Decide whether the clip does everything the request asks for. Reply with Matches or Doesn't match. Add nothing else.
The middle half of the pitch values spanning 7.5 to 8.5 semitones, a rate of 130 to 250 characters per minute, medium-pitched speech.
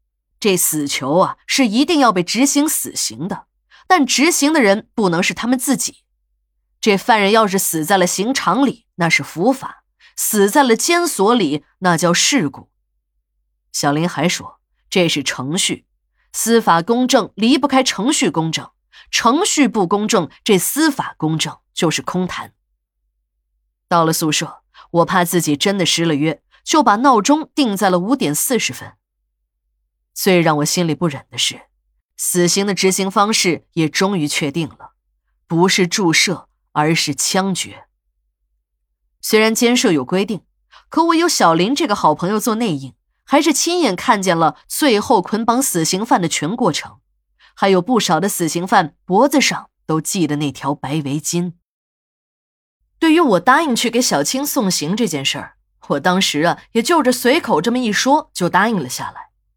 Matches